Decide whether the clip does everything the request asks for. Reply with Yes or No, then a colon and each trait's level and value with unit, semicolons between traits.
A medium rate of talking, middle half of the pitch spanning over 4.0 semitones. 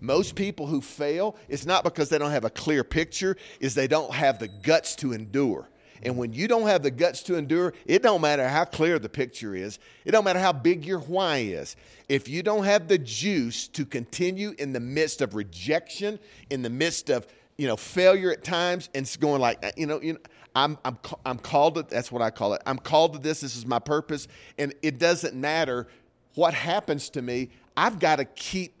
No: fast, 220 wpm; average, 5.1 semitones